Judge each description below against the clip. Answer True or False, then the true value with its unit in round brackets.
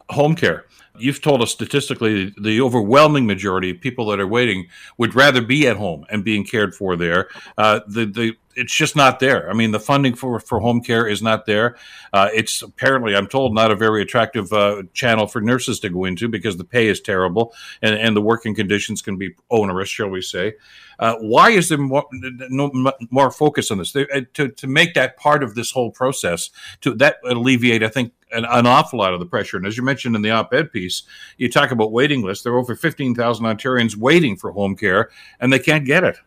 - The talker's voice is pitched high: False (115 Hz)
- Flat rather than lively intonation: False (3.5 semitones)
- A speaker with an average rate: False (220 wpm)